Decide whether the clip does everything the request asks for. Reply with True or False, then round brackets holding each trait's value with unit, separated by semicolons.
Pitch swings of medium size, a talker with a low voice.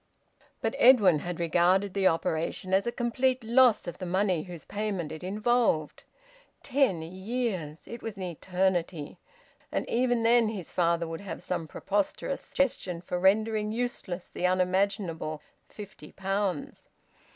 False (4.2 semitones; 190 Hz)